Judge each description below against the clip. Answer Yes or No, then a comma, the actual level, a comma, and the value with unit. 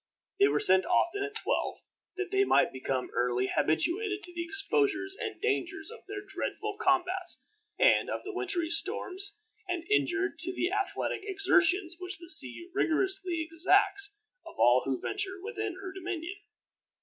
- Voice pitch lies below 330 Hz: No, very high, 380 Hz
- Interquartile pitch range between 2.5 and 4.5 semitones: Yes, average, 2.8 semitones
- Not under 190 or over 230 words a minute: No, average, 155 wpm